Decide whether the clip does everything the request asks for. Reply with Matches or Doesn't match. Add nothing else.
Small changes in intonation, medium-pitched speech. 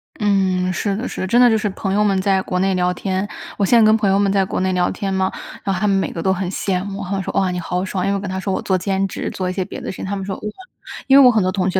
Doesn't match